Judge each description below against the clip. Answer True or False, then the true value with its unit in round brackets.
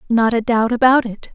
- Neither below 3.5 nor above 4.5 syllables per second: False (5.2 syllables/s)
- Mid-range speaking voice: False (235 Hz)